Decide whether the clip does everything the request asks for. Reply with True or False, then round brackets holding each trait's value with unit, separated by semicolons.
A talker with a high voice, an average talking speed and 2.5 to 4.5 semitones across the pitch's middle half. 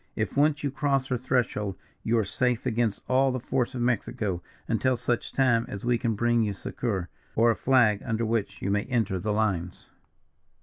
False (115 Hz; 190 wpm; 3.2 semitones)